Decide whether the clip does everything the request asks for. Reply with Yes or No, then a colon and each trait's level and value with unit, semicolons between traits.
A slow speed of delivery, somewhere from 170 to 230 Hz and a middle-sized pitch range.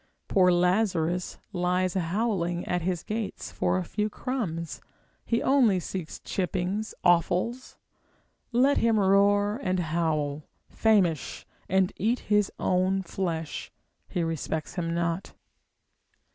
Yes: slow, 115 wpm; medium, 185 Hz; average, 3.4 semitones